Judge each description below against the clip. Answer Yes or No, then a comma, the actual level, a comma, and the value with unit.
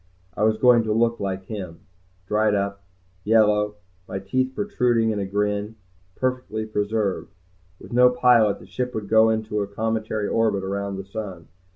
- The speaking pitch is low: Yes, low, 110 Hz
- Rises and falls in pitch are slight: Yes, narrow, 2.1 semitones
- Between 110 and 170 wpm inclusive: Yes, average, 165 wpm